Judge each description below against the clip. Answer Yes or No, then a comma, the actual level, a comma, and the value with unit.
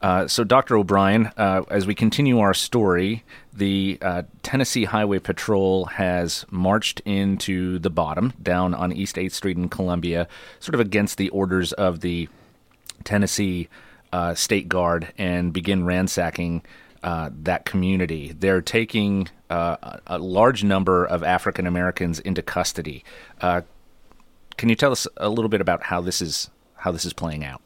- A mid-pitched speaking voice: No, very low, 95 Hz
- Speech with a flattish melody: Yes, narrow, 2.3 semitones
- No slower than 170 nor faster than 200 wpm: No, average, 155 wpm